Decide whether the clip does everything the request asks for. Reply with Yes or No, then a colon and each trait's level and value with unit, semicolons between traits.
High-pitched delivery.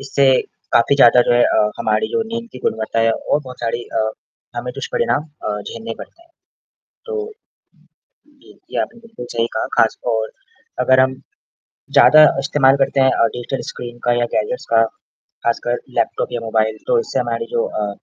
No: low, 125 Hz